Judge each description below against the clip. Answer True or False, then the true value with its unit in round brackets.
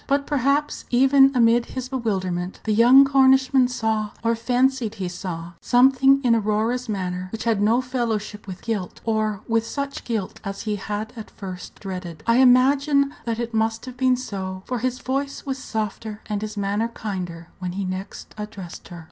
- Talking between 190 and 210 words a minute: False (175 wpm)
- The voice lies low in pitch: False (225 Hz)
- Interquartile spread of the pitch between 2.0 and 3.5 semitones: False (4.2 semitones)